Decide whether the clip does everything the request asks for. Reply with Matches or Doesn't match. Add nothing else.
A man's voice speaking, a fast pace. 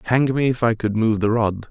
Matches